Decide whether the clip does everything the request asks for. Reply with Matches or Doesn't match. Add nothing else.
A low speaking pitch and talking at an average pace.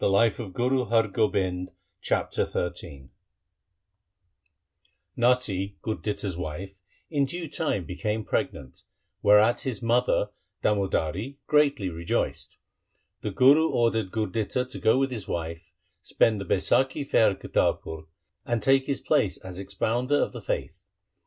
Doesn't match